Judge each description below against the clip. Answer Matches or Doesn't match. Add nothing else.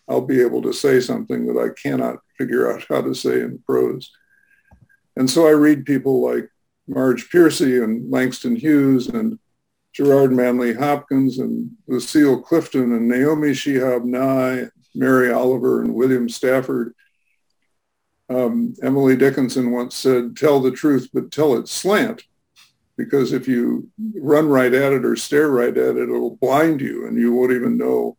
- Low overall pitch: Matches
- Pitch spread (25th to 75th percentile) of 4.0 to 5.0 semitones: Doesn't match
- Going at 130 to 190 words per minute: Matches